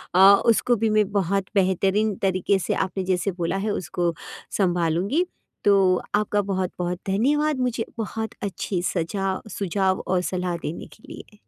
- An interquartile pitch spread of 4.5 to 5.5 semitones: No, average, 2.8 semitones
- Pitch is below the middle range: No, high, 195 Hz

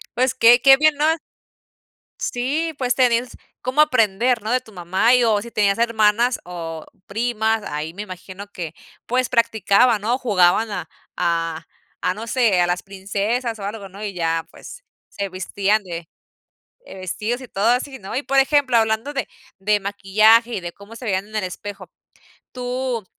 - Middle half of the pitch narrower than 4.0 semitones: No, average, 4.3 semitones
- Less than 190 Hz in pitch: No, high, 215 Hz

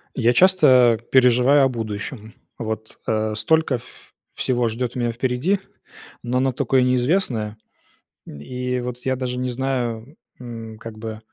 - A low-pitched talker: Yes, low, 125 Hz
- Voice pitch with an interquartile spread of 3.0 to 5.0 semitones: No, narrow, 2.4 semitones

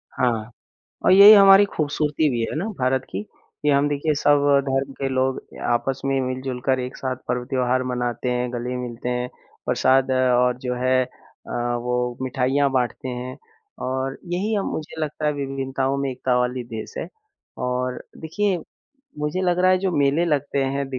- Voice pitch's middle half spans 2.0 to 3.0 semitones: Yes, narrow, 2.6 semitones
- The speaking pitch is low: Yes, low, 130 Hz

